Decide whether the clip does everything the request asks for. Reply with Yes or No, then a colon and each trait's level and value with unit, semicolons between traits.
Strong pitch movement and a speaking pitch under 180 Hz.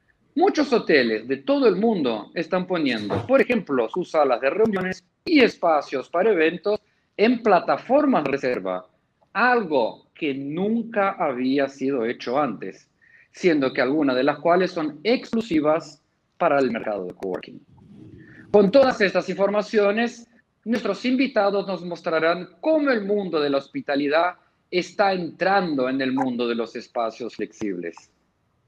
No: wide, 6.9 semitones; medium, 185 Hz